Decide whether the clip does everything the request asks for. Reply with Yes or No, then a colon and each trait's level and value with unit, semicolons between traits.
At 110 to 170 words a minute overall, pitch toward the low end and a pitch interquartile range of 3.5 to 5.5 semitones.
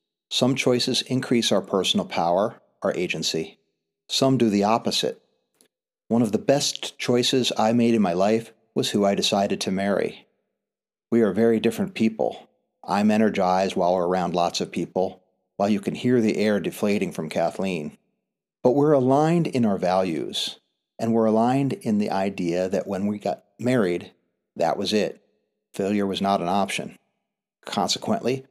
Yes: average, 160 wpm; low, 110 Hz; average, 4.1 semitones